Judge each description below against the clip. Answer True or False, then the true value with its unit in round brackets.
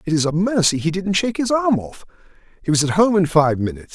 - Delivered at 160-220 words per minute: False (260 wpm)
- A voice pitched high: False (175 Hz)